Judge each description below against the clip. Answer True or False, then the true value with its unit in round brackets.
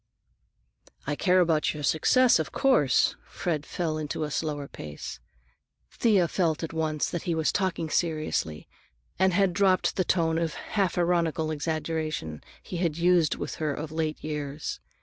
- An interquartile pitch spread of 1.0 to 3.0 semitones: True (2.6 semitones)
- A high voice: False (160 Hz)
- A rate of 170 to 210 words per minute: False (155 wpm)